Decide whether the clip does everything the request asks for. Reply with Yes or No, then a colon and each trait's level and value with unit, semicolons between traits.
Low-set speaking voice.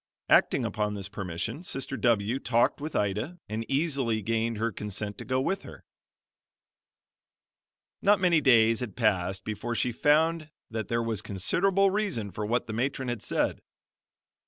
Yes: low, 115 Hz